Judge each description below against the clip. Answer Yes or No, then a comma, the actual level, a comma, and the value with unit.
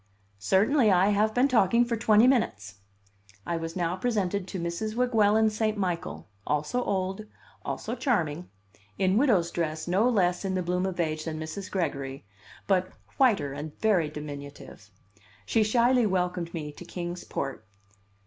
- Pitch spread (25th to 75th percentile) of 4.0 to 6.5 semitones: Yes, average, 4.8 semitones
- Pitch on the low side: No, medium, 185 Hz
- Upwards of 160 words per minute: No, average, 150 wpm